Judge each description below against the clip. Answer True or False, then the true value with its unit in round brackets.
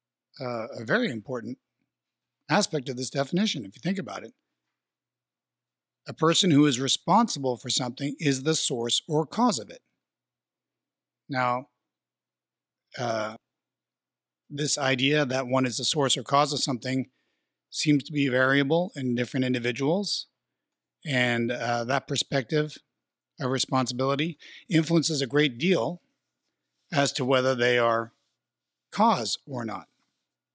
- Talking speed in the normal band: False (130 wpm)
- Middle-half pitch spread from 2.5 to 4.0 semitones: True (3.1 semitones)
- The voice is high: False (140 Hz)